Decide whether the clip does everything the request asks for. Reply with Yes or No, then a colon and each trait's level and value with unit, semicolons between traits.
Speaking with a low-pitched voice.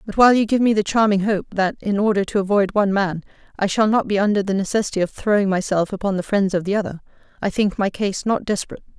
No: high, 200 Hz